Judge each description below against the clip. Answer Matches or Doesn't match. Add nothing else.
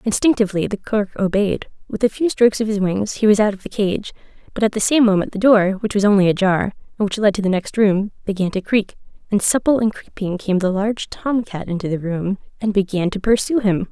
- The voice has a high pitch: Matches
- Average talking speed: Doesn't match